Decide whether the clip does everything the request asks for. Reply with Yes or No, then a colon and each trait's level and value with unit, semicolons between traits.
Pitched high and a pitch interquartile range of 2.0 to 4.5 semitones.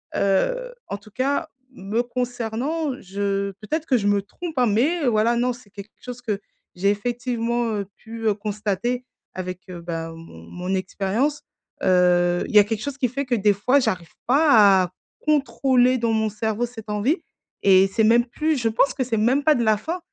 Yes: high, 225 Hz; average, 4.0 semitones